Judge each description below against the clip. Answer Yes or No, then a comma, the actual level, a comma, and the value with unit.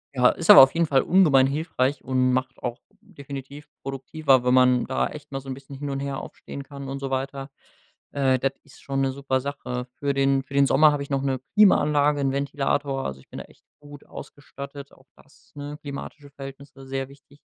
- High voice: No, medium, 140 Hz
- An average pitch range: No, narrow, 1.1 semitones